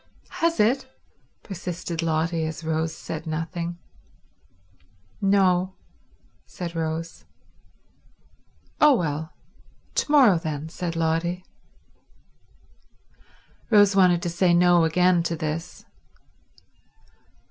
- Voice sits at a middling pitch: Yes, medium, 170 Hz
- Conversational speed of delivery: No, slow, 85 wpm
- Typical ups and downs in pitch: No, narrow, 2.2 semitones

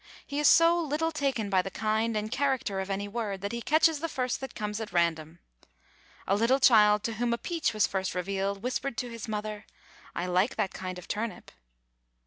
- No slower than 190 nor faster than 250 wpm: Yes, fast, 205 wpm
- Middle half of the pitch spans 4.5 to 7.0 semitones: Yes, average, 4.8 semitones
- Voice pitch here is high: Yes, high, 215 Hz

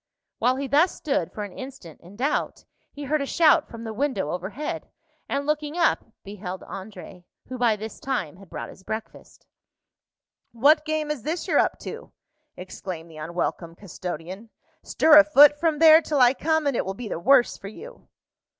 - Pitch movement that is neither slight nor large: No, wide, 7.7 semitones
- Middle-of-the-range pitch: No, very high, 250 Hz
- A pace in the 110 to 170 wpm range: No, average, 185 wpm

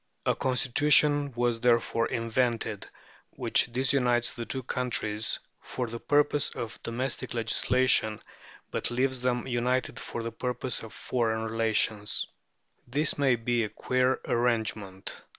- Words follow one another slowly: Yes, slow, 125 wpm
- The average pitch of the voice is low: Yes, low, 120 Hz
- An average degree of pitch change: No, narrow, 2.1 semitones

